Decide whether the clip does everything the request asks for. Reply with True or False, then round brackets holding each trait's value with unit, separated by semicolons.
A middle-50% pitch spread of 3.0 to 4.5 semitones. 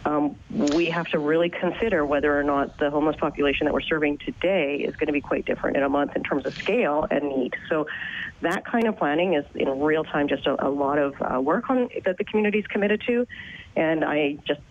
True (3.7 semitones)